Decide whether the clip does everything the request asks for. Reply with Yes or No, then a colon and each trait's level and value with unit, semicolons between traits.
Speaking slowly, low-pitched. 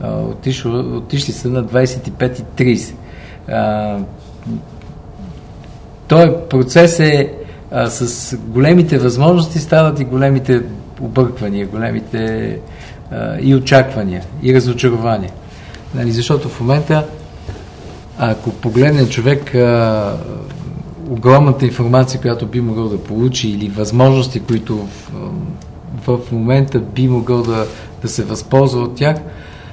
Yes: slow, 110 wpm; low, 125 Hz